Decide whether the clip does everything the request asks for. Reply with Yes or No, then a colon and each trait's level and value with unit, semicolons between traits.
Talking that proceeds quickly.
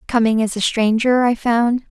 No: average, 185 wpm